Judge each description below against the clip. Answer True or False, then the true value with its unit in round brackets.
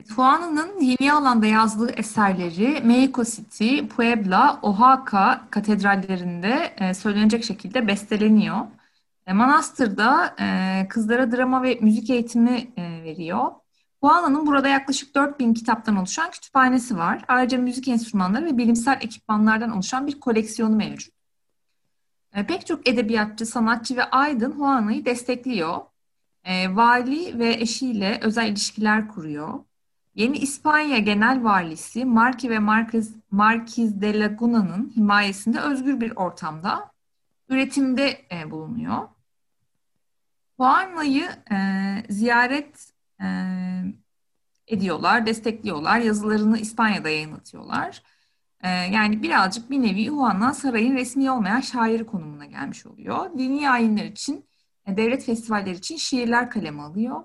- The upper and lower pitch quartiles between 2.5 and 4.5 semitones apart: True (3.5 semitones)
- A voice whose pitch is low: False (230 Hz)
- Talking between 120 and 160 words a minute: False (105 wpm)